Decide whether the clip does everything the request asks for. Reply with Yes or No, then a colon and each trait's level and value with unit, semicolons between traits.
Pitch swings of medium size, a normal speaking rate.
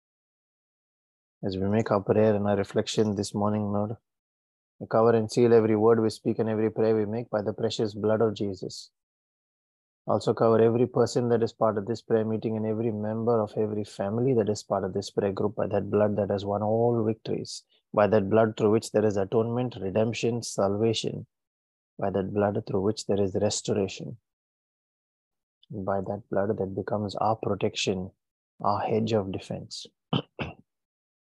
No: narrow, 2.0 semitones; average, 170 wpm